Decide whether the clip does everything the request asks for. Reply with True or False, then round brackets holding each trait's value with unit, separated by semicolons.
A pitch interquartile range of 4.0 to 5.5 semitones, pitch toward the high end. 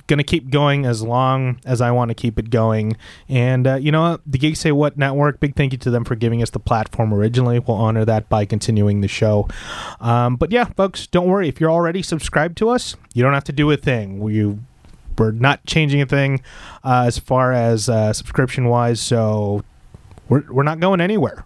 False (4.6 semitones; 125 Hz)